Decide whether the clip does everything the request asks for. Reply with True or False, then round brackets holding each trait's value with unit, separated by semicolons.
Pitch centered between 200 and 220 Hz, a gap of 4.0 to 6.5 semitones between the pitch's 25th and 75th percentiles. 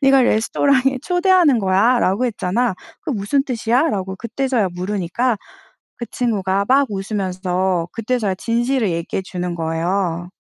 True (210 Hz; 5.2 semitones)